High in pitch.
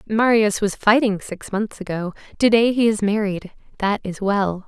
Yes: high, 205 Hz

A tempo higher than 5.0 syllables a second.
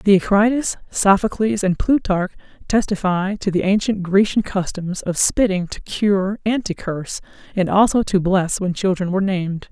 No: 4.7 syllables/s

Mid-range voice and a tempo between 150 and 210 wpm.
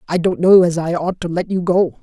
No: medium, 175 Hz; fast, 295 wpm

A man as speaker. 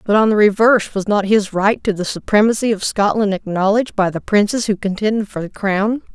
No: female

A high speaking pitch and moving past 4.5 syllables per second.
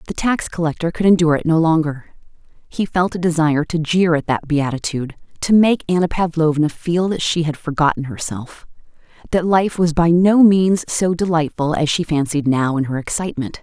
No: medium, 160 Hz; 5.4 syllables/s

